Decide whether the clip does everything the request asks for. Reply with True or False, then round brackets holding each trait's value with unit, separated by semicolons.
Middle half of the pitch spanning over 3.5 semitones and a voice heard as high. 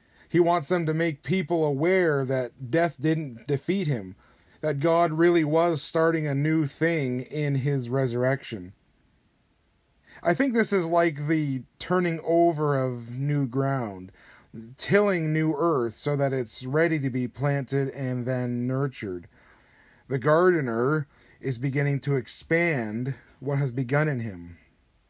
False (4.3 semitones; 140 Hz)